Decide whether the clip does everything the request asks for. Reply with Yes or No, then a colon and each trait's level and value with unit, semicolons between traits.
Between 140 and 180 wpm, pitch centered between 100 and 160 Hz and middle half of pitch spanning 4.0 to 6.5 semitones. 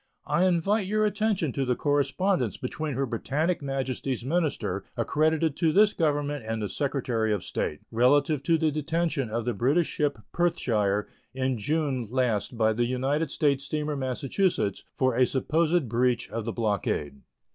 Yes: average, 155 wpm; medium, 140 Hz; average, 4.9 semitones